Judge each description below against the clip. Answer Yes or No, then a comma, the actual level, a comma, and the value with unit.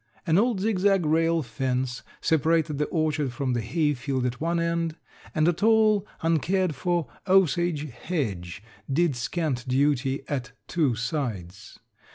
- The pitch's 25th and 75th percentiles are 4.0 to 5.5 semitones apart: Yes, average, 5.0 semitones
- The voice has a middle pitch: Yes, medium, 155 Hz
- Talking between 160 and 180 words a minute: No, average, 140 wpm